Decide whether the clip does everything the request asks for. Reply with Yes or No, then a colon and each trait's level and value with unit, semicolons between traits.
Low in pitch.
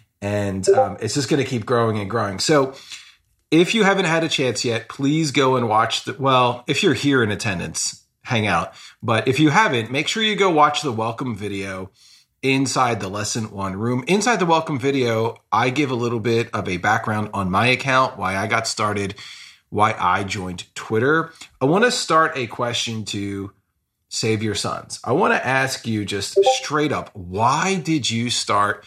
Yes: low, 120 Hz